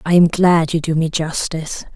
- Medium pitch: Yes, medium, 165 Hz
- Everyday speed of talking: No, fast, 215 wpm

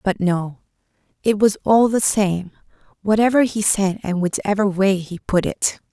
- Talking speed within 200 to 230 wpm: No, average, 160 wpm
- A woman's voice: Yes, female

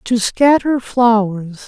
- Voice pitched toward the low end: No, high, 230 Hz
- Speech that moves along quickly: No, slow, 110 wpm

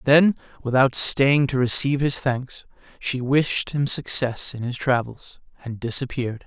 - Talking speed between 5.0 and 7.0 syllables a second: No, 4.4 syllables/s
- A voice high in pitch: No, low, 130 Hz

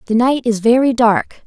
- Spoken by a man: No, female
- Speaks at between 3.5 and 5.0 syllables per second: Yes, 4.8 syllables/s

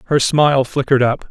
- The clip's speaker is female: No, male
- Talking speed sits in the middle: Yes, average, 185 wpm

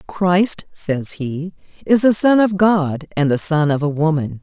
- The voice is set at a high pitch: No, medium, 170 Hz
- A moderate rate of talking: Yes, average, 190 wpm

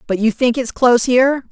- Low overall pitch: No, high, 245 Hz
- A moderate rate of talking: No, fast, 240 wpm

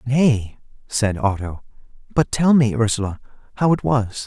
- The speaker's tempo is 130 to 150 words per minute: Yes, average, 140 wpm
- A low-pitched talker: Yes, low, 115 Hz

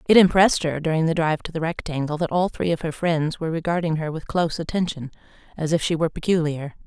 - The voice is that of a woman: Yes, female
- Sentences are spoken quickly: Yes, fast, 225 wpm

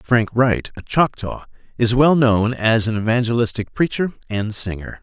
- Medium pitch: No, low, 115 Hz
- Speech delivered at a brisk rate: No, average, 155 wpm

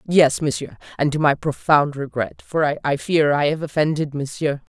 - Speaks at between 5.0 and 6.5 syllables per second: No, 4.8 syllables/s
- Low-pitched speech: No, medium, 150 Hz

